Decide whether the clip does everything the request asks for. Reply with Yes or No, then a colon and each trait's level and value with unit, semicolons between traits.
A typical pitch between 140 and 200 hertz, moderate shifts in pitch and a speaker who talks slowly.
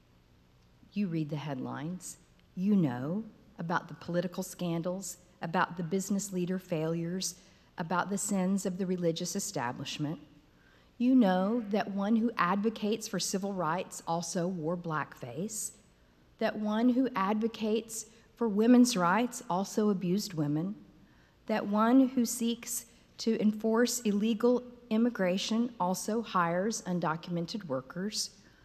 Yes: high, 190 Hz; average, 4.2 semitones; slow, 115 wpm